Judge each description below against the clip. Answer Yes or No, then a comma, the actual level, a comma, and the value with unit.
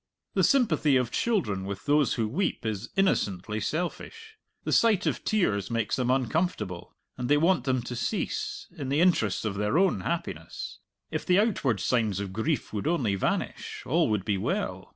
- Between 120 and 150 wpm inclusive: No, average, 175 wpm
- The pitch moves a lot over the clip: Yes, wide, 8.6 semitones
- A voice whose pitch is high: No, low, 130 Hz